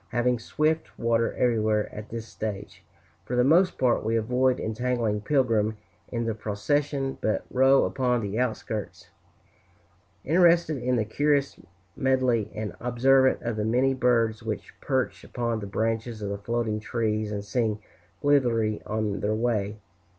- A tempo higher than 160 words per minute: No, average, 145 wpm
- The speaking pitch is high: No, low, 115 Hz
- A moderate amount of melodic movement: Yes, average, 3.1 semitones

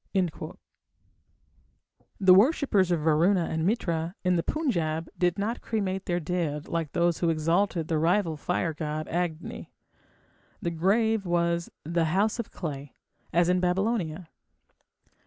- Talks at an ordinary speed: No, slow, 130 wpm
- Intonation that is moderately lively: Yes, average, 3.0 semitones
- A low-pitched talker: No, medium, 175 Hz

